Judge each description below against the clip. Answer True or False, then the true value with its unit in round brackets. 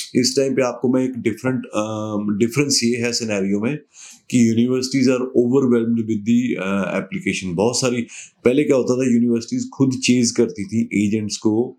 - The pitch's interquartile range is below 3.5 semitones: True (2.8 semitones)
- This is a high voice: False (120 Hz)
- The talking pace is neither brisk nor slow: True (170 wpm)